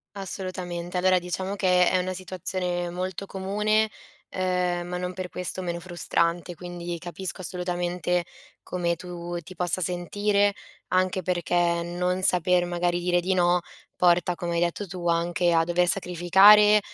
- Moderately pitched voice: Yes, medium, 180 Hz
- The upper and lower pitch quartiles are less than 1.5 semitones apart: Yes, narrow, 1.1 semitones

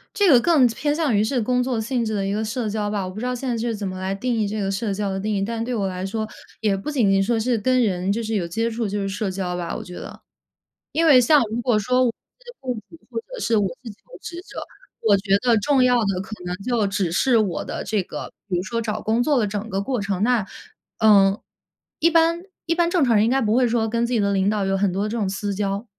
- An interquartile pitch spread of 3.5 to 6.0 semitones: Yes, average, 4.0 semitones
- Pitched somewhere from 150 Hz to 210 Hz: No, high, 220 Hz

